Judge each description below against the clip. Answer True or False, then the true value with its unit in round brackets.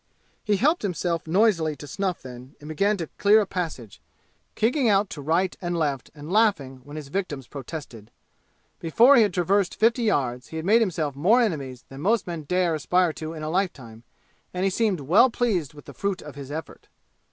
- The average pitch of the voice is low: False (170 Hz)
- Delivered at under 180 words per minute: False (195 wpm)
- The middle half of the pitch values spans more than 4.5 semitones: True (5.5 semitones)